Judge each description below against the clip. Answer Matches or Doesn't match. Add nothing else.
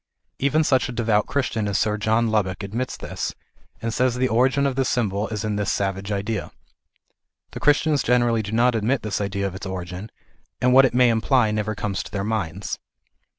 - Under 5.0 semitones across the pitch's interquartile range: Matches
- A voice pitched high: Doesn't match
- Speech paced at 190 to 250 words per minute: Matches